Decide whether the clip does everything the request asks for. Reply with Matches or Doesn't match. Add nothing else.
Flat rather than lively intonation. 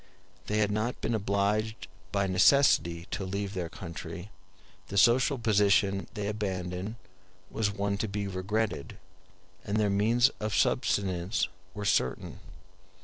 Matches